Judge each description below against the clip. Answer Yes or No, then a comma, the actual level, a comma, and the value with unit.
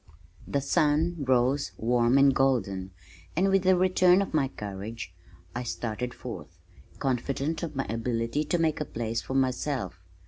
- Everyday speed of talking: Yes, average, 150 wpm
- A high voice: No, low, 130 Hz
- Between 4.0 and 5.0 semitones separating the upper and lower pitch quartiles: Yes, average, 4.7 semitones